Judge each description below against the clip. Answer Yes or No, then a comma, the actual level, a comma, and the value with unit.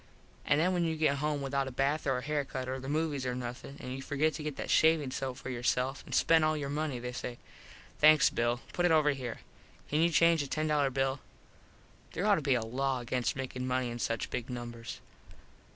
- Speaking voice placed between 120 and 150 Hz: Yes, low, 135 Hz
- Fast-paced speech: Yes, fast, 230 wpm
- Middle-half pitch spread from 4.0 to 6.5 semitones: No, average, 3.3 semitones